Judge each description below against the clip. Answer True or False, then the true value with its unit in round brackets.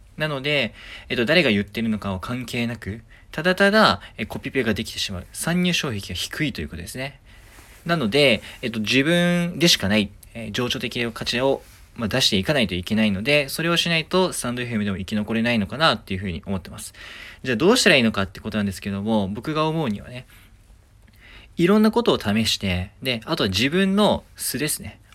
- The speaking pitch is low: True (110 Hz)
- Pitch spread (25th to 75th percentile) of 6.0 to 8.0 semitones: False (5.2 semitones)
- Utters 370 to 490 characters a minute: True (405 characters per minute)